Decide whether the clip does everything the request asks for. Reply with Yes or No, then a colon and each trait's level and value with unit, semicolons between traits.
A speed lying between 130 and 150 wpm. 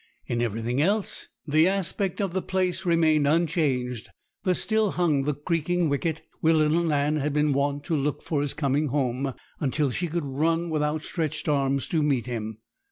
No: average, 175 wpm